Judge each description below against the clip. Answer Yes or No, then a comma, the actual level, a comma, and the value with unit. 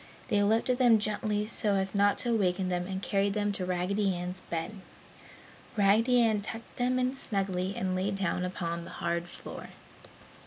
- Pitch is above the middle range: Yes, high, 200 Hz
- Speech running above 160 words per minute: Yes, average, 170 wpm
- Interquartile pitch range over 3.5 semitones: No, average, 2.7 semitones